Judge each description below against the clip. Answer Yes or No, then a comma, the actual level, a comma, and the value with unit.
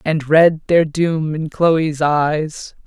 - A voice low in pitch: No, medium, 155 Hz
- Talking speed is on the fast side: No, average, 145 wpm